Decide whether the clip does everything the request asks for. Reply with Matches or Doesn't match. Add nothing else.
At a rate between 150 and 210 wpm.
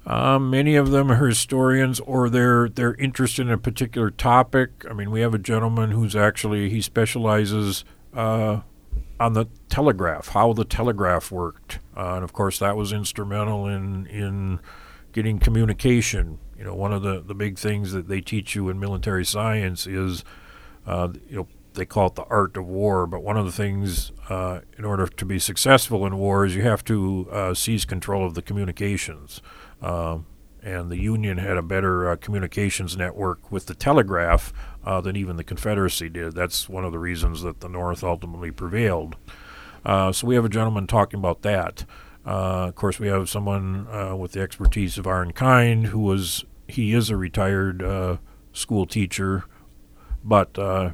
Matches